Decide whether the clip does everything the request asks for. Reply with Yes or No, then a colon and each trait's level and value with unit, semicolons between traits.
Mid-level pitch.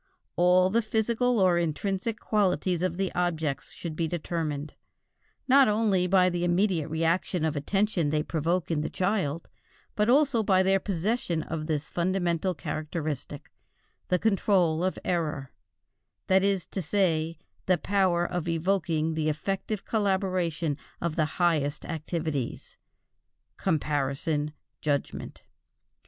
Yes: medium, 175 Hz